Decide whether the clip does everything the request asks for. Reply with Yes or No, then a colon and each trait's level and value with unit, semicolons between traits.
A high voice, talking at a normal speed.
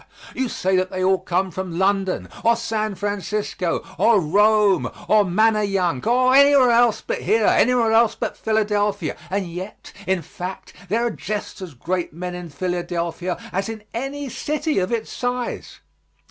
Yes: high, 205 Hz; average, 160 wpm